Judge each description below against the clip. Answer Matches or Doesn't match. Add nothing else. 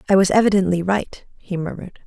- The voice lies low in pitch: Doesn't match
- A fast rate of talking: Doesn't match